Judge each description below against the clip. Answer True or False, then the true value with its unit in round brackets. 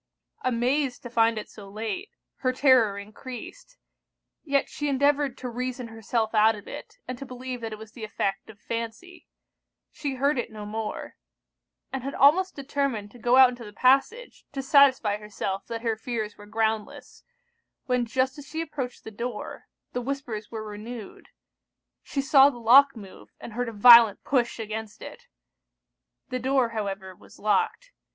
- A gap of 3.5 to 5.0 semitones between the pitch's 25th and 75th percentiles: True (3.8 semitones)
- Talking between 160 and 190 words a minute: True (170 wpm)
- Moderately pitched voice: False (240 Hz)